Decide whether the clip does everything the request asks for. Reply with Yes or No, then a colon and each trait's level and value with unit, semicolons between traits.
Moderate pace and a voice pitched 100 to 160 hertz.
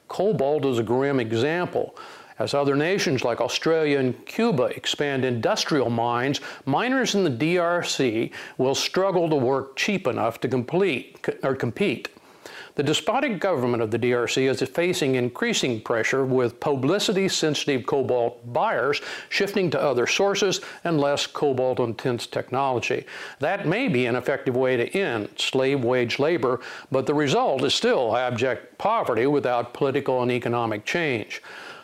Yes: average, 145 wpm; low, 135 Hz